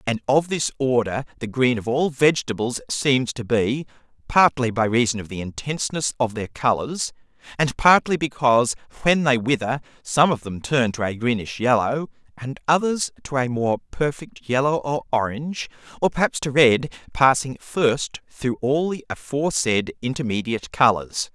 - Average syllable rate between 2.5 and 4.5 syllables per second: No, 4.8 syllables/s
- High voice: No, low, 130 Hz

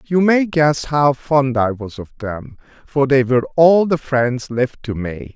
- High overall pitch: No, low, 135 Hz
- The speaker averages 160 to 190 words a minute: No, average, 200 wpm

